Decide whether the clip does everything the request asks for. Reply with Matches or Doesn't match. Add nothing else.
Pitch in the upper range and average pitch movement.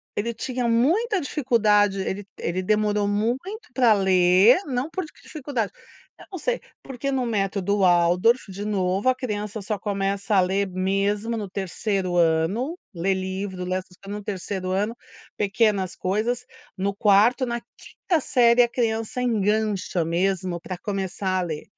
Matches